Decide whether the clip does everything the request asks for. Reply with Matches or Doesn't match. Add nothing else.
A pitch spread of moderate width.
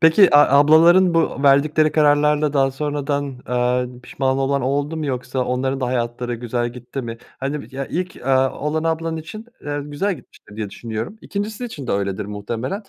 Matches